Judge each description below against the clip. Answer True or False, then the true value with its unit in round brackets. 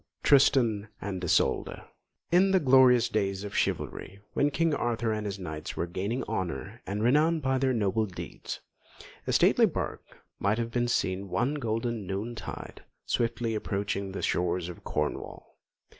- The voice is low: True (110 Hz)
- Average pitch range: True (4.2 semitones)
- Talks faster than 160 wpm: False (155 wpm)